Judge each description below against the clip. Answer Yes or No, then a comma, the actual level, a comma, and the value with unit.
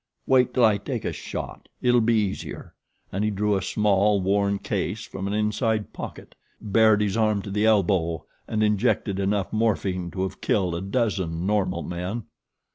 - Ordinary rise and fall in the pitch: No, narrow, 2.0 semitones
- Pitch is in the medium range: No, low, 100 Hz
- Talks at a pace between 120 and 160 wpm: No, average, 175 wpm